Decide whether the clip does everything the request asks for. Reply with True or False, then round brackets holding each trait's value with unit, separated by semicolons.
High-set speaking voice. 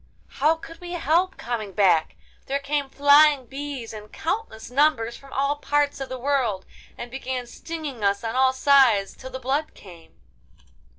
True (270 Hz)